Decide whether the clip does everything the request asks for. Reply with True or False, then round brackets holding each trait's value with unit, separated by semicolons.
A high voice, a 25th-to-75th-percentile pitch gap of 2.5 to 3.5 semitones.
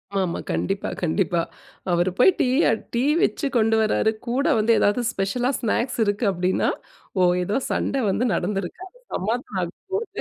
False (210 Hz; 4.5 semitones)